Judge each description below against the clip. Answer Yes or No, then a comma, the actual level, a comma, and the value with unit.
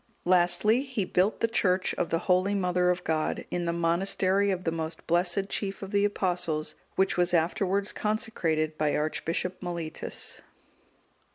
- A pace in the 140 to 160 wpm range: Yes, average, 155 wpm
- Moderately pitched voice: Yes, medium, 180 Hz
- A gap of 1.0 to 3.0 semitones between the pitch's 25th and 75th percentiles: Yes, average, 2.7 semitones